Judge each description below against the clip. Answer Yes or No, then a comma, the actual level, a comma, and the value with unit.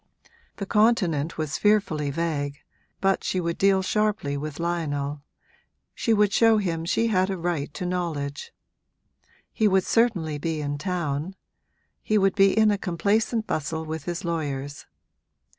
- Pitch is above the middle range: No, medium, 175 Hz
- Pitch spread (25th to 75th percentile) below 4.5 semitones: No, average, 4.9 semitones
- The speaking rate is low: No, average, 145 wpm